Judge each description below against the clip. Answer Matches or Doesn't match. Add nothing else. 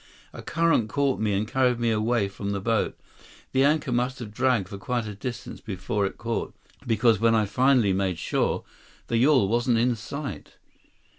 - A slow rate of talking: Doesn't match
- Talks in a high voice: Doesn't match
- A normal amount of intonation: Matches